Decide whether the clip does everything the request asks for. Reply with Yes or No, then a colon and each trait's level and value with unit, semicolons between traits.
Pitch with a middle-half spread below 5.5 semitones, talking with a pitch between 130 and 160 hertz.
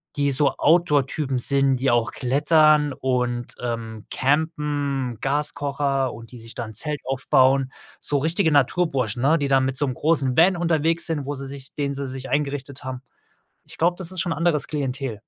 Yes: narrow, 2.5 semitones; medium, 140 Hz